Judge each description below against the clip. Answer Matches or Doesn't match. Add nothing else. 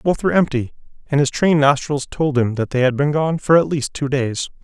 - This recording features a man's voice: Matches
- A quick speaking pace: Matches